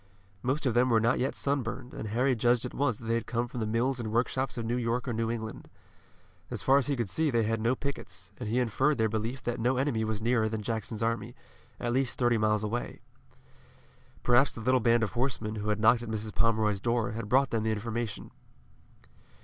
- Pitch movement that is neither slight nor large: No, narrow, 2.3 semitones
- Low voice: Yes, low, 115 Hz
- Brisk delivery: Yes, fast, 225 wpm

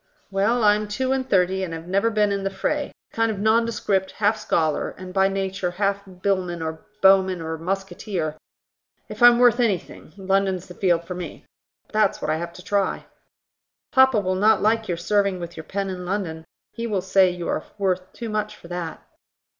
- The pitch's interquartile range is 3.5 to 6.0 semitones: No, average, 2.9 semitones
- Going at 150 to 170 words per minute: No, average, 195 wpm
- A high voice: Yes, high, 195 Hz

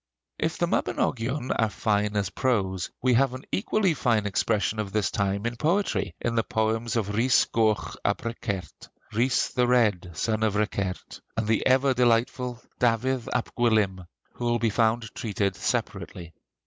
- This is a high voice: No, low, 115 Hz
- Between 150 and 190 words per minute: Yes, average, 160 wpm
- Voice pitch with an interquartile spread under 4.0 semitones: Yes, average, 3.1 semitones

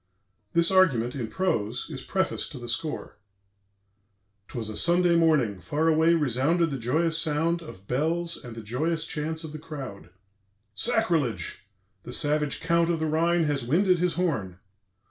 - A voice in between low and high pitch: Yes, medium, 155 Hz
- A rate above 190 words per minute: No, average, 155 wpm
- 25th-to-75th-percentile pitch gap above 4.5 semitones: Yes, average, 5.3 semitones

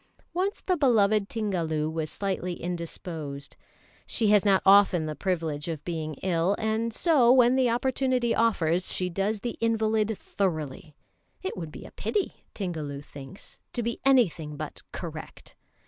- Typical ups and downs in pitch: No, wide, 6.0 semitones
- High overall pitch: Yes, high, 195 Hz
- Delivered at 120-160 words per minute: Yes, average, 145 wpm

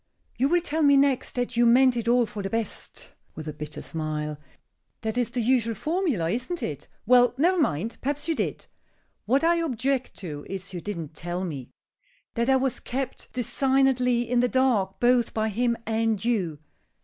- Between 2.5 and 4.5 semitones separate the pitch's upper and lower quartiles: No, average, 4.9 semitones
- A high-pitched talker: Yes, high, 240 Hz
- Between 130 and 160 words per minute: No, average, 185 wpm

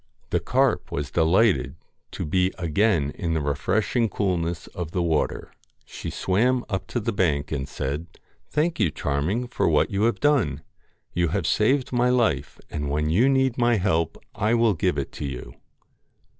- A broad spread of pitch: Yes, wide, 7.3 semitones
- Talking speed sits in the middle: Yes, average, 175 wpm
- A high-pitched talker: No, very low, 90 Hz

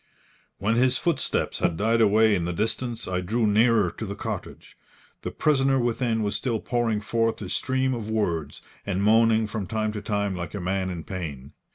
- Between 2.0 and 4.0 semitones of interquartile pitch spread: Yes, average, 3.1 semitones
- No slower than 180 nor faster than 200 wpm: Yes, average, 190 wpm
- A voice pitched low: Yes, low, 110 Hz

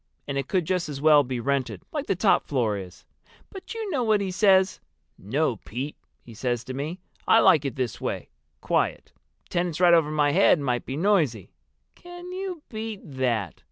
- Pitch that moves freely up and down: Yes, wide, 7.5 semitones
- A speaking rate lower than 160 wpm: No, average, 185 wpm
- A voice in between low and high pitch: Yes, medium, 150 Hz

